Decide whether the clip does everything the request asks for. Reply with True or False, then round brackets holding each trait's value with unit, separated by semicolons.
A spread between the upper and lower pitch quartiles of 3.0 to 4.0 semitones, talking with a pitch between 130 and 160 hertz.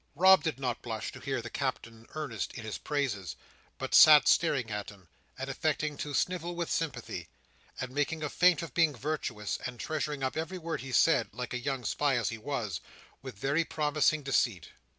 False (4.6 semitones; 140 Hz)